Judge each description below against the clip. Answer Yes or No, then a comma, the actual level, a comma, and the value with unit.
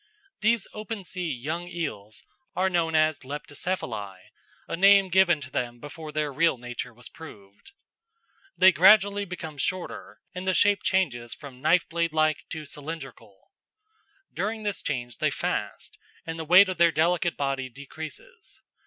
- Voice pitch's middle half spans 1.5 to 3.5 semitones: No, average, 5.3 semitones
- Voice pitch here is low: No, medium, 160 Hz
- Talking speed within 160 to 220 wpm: No, average, 150 wpm